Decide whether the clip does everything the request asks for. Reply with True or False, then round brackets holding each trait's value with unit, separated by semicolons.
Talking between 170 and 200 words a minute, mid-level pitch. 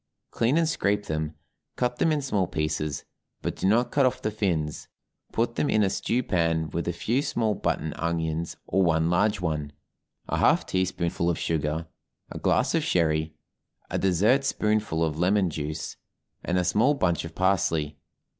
False (175 wpm; 90 Hz)